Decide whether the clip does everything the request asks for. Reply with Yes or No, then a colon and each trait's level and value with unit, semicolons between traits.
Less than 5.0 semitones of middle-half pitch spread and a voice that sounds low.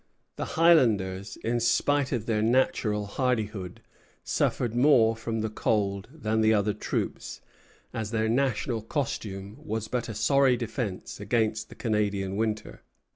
Yes: narrow, 2.5 semitones; low, 110 Hz